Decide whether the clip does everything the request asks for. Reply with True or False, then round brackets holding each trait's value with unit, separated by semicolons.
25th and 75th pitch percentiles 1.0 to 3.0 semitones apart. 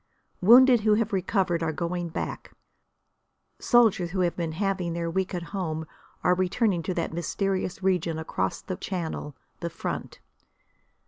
True (2.5 semitones)